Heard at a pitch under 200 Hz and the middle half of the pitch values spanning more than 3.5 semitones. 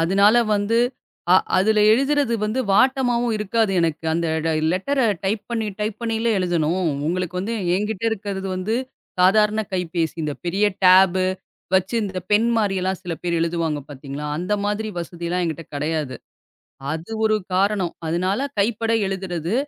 Yes: high, 190 Hz; average, 4.0 semitones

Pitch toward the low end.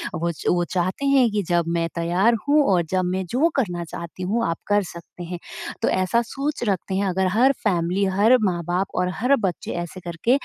No: medium, 185 Hz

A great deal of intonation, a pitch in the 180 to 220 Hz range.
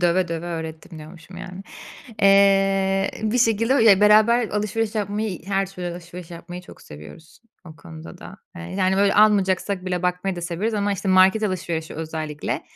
No: average, 2.9 semitones; medium, 185 Hz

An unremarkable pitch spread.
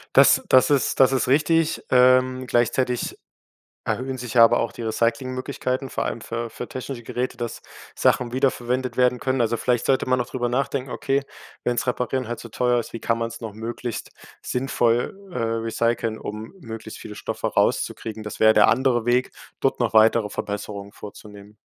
No: narrow, 2.1 semitones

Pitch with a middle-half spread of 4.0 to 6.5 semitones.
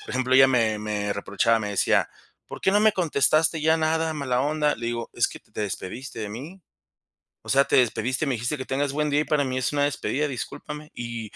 Yes: average, 4.4 semitones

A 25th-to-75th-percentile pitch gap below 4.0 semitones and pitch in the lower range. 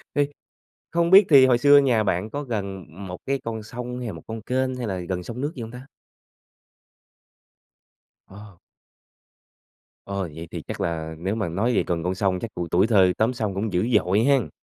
No: average, 5.2 semitones; low, 110 Hz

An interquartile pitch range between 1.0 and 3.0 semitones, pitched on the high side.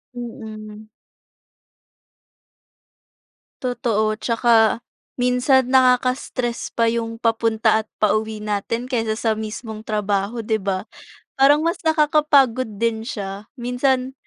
Yes: average, 2.7 semitones; high, 230 Hz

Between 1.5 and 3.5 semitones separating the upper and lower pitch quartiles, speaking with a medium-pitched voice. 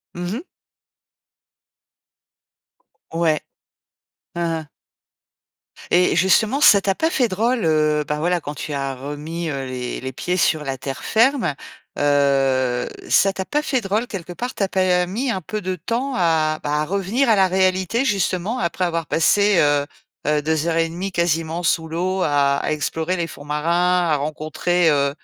No: average, 4.2 semitones; medium, 170 Hz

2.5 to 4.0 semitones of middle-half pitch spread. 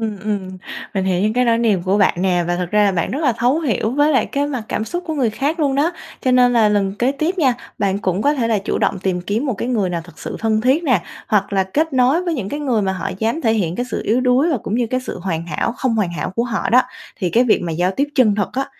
No: average, 5.3 semitones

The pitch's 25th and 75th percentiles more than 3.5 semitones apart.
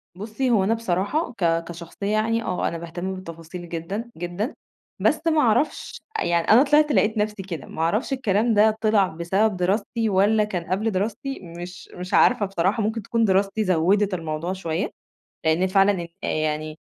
Yes: average, 4.1 semitones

